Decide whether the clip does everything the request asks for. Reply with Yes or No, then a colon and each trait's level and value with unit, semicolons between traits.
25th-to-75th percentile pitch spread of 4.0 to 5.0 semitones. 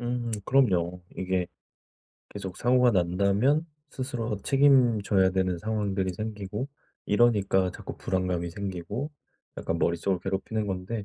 Yes: average, 4.3 semitones